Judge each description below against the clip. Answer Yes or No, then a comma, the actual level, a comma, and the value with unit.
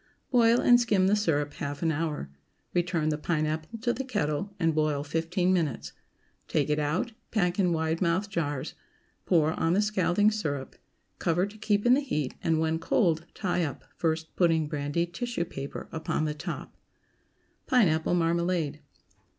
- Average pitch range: Yes, average, 4.0 semitones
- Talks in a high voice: No, medium, 165 Hz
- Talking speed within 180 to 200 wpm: No, average, 160 wpm